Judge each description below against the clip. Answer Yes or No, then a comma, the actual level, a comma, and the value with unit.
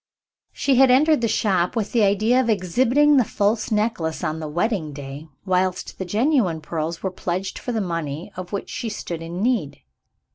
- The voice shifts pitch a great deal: Yes, wide, 5.7 semitones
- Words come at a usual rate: Yes, average, 185 wpm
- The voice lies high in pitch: Yes, high, 195 Hz